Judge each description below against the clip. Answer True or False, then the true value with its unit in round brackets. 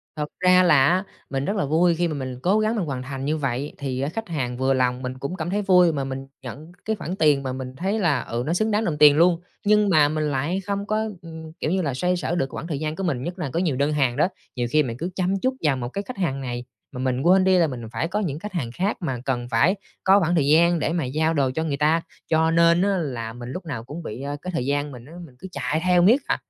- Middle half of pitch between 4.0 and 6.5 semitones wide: True (5.1 semitones)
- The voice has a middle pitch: True (155 Hz)